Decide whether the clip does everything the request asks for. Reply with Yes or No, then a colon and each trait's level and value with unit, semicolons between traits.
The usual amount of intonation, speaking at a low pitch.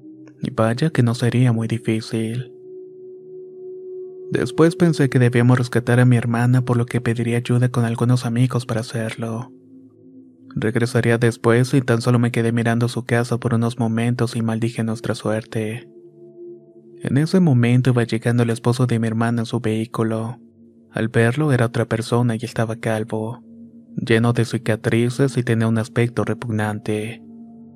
No: narrow, 2.1 semitones; low, 120 Hz